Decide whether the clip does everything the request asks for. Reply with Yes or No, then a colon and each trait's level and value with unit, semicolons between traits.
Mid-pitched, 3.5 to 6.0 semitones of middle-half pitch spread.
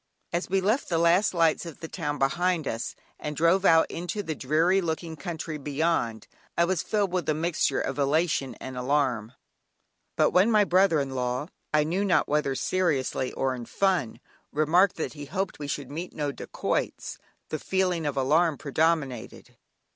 Yes: medium, 160 Hz; average, 4.1 semitones